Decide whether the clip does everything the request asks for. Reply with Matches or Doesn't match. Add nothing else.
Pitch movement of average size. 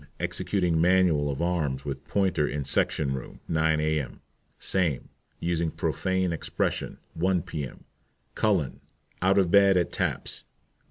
Matches